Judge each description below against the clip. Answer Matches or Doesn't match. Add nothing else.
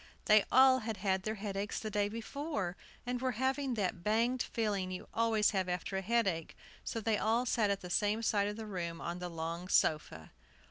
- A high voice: Matches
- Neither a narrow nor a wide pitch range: Matches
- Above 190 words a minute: Matches